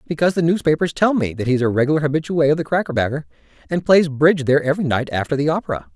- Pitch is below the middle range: No, medium, 150 Hz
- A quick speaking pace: Yes, fast, 230 wpm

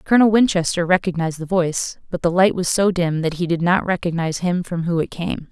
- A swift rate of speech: Yes, fast, 230 wpm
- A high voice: No, medium, 175 Hz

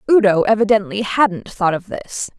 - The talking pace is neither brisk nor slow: Yes, average, 150 wpm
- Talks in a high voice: Yes, high, 205 Hz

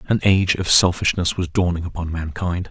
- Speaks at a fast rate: No, average, 180 wpm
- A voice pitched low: Yes, very low, 90 Hz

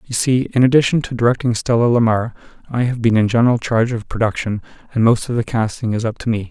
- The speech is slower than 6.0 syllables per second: No, 6.5 syllables/s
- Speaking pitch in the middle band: No, low, 115 Hz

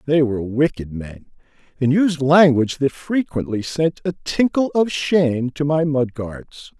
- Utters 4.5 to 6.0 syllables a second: No, 4.3 syllables/s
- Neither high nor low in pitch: Yes, medium, 145 Hz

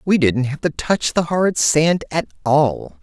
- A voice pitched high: No, medium, 145 Hz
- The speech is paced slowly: No, average, 200 wpm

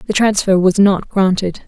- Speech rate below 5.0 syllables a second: Yes, 4.8 syllables/s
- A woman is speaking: Yes, female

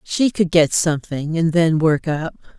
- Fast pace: No, average, 185 wpm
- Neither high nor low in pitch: Yes, medium, 165 Hz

